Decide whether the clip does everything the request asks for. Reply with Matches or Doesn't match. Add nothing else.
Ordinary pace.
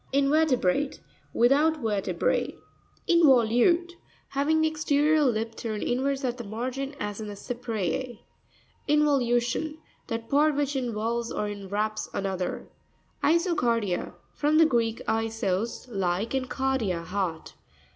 Doesn't match